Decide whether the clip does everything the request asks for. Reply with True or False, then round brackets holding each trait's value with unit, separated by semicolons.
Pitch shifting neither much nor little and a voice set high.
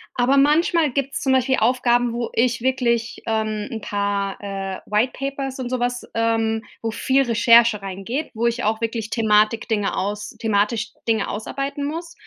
True (3.2 semitones; 230 Hz)